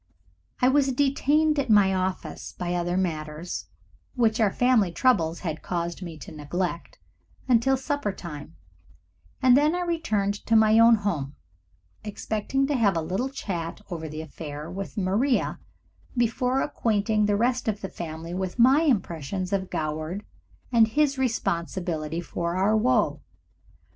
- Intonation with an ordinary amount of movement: No, wide, 6.5 semitones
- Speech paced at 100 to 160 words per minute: Yes, average, 145 wpm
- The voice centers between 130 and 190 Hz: No, high, 200 Hz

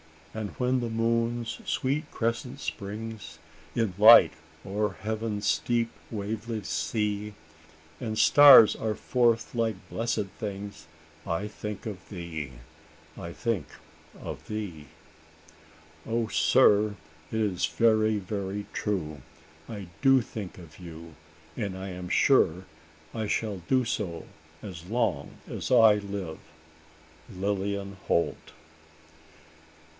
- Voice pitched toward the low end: Yes, low, 105 Hz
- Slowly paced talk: Yes, slow, 110 wpm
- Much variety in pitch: No, average, 3.2 semitones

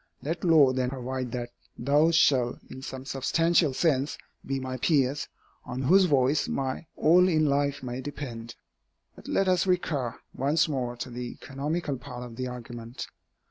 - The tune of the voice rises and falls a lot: No, average, 3.5 semitones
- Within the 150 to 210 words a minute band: Yes, average, 160 wpm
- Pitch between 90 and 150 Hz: Yes, low, 135 Hz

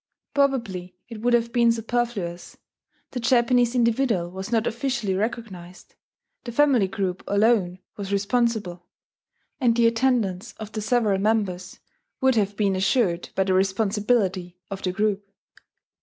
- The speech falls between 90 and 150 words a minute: Yes, slow, 135 wpm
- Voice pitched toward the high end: Yes, high, 215 Hz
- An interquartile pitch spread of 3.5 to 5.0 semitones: Yes, average, 3.8 semitones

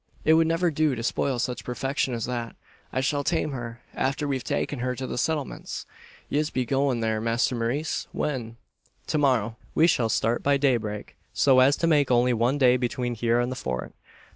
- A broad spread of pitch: No, average, 3.2 semitones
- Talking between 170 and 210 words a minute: Yes, average, 195 wpm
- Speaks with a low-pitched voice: Yes, low, 130 Hz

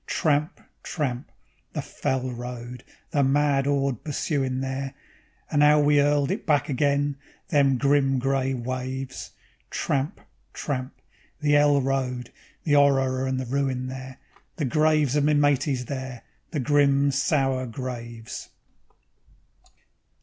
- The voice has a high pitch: No, low, 135 Hz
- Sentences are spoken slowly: Yes, slow, 125 wpm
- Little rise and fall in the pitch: Yes, narrow, 1.9 semitones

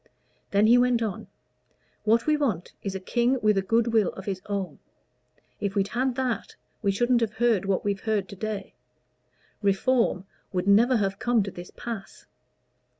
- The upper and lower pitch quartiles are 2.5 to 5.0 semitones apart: Yes, average, 3.4 semitones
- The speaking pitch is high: Yes, high, 215 Hz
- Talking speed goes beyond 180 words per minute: No, average, 175 wpm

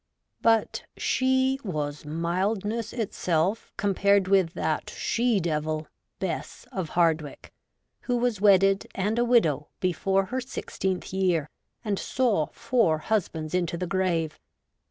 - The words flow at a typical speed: No, slow, 120 wpm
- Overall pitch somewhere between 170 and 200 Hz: Yes, high, 190 Hz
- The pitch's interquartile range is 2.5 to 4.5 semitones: No, average, 5.2 semitones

